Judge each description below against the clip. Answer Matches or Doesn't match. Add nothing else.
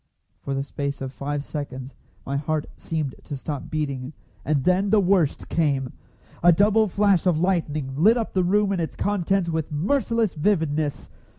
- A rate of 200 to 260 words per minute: Doesn't match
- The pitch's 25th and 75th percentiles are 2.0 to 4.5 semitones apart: Doesn't match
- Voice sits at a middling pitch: Matches